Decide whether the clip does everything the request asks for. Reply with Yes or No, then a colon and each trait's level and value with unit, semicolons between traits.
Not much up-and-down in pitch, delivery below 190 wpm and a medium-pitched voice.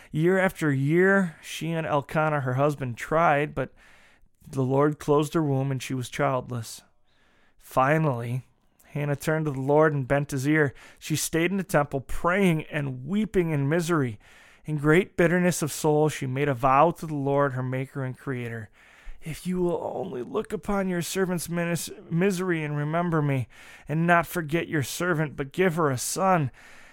No: average, 3.7 semitones; average, 170 wpm; medium, 150 Hz